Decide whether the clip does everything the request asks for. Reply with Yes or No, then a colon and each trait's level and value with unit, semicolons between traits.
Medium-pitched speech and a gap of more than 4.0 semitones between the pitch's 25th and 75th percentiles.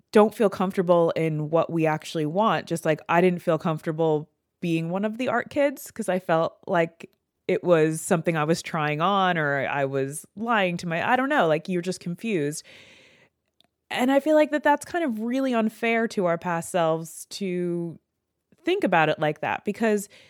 Yes: medium, 180 Hz; average, 5.3 semitones